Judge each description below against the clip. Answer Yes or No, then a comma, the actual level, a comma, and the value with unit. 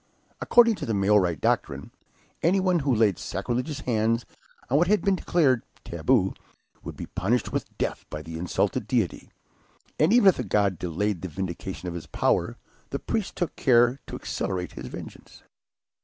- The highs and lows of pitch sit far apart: Yes, wide, 8.7 semitones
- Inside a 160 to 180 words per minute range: Yes, average, 165 wpm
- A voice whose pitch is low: Yes, low, 110 Hz